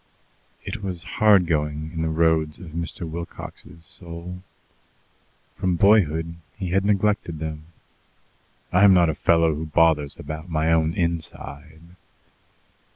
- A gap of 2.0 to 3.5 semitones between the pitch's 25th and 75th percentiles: Yes, narrow, 2.4 semitones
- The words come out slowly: Yes, slow, 130 wpm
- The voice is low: Yes, very low, 85 Hz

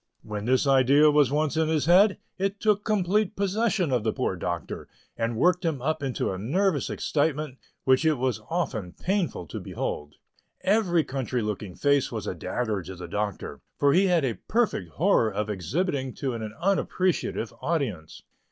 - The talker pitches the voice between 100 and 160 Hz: Yes, medium, 140 Hz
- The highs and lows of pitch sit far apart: Yes, wide, 8.3 semitones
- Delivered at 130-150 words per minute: No, average, 170 wpm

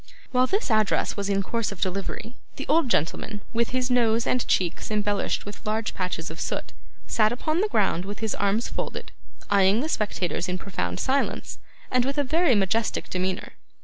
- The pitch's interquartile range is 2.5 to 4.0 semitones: No, average, 4.4 semitones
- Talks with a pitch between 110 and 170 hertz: No, high, 215 Hz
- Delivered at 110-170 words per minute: No, average, 180 wpm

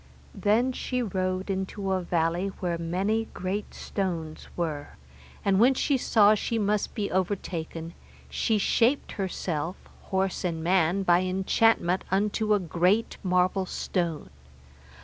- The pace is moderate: No, slow, 130 wpm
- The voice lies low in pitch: No, high, 190 Hz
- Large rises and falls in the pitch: No, average, 3.1 semitones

